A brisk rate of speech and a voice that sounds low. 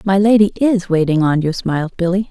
No: fast, 210 wpm; medium, 185 Hz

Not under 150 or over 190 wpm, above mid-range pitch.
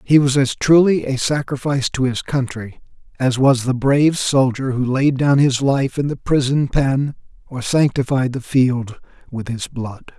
No: average, 175 wpm; low, 135 Hz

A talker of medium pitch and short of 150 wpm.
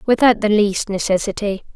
No: high, 210 Hz; slow, 135 wpm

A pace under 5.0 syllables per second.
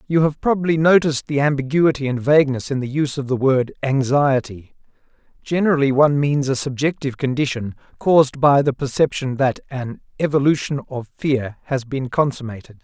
No: 5.6 syllables/s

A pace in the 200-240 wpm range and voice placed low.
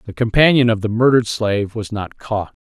Yes: fast, 205 wpm; low, 110 Hz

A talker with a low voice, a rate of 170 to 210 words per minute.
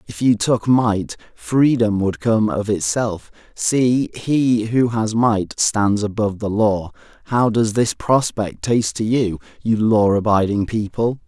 No: low, 110 Hz; average, 155 wpm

